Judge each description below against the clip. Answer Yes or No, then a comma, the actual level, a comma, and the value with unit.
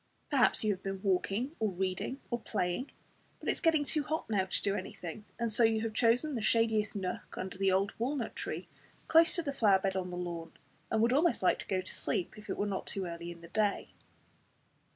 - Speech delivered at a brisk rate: Yes, fast, 230 wpm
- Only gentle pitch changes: No, average, 4.2 semitones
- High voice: Yes, high, 210 Hz